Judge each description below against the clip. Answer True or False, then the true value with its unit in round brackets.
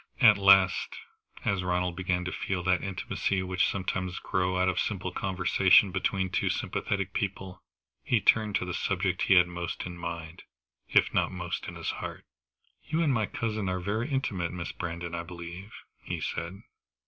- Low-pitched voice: True (95 Hz)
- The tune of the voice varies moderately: False (1.8 semitones)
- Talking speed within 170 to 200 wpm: True (175 wpm)